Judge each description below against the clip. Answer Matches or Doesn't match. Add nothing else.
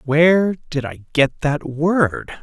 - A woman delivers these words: Doesn't match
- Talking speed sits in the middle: Matches